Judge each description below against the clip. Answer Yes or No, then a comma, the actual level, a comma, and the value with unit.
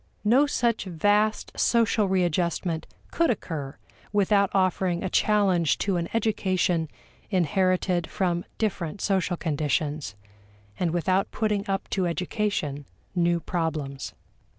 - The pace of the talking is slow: Yes, slow, 110 wpm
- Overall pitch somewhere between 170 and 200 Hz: Yes, medium, 185 Hz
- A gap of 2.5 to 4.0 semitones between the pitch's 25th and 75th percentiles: Yes, average, 3.5 semitones